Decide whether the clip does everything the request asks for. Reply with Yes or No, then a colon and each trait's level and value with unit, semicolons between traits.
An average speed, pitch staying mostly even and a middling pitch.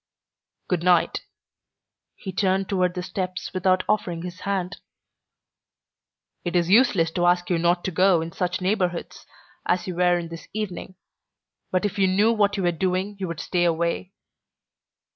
Yes: average, 160 wpm; narrow, 1.5 semitones; medium, 180 Hz